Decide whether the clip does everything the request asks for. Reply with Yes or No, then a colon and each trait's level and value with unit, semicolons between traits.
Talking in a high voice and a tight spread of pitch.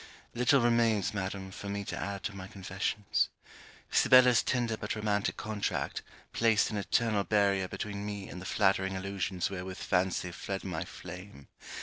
No: low, 100 Hz; narrow, 2.1 semitones